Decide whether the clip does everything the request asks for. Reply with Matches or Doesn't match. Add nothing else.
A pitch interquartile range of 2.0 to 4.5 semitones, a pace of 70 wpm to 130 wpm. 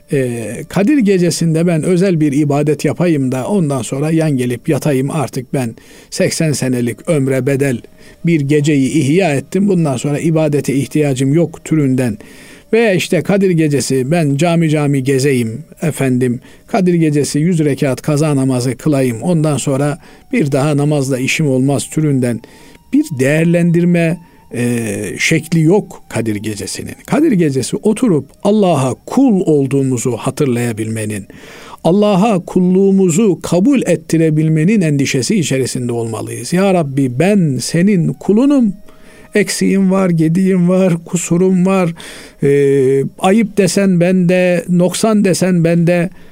Doesn't match